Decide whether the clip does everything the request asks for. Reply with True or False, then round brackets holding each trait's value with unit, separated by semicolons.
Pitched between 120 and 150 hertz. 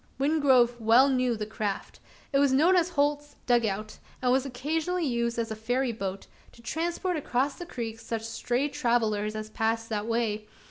False (240 Hz)